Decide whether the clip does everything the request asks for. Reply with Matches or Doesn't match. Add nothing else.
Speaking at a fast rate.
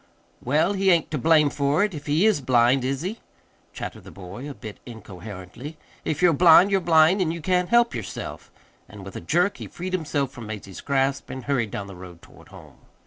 Matches